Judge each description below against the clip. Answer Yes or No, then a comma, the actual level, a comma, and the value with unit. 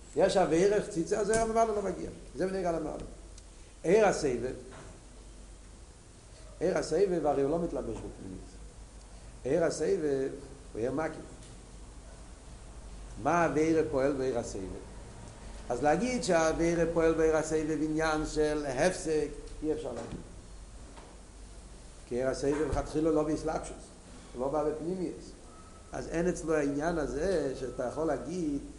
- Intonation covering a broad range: Yes, wide, 6.9 semitones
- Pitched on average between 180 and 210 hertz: No, medium, 155 Hz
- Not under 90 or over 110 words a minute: Yes, slow, 100 wpm